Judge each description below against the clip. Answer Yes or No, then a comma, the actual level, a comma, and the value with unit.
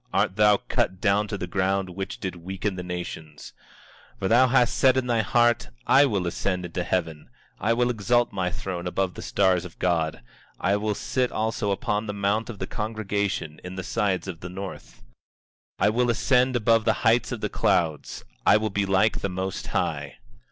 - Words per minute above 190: Yes, average, 200 wpm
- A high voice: No, low, 100 Hz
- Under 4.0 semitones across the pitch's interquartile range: Yes, average, 3.5 semitones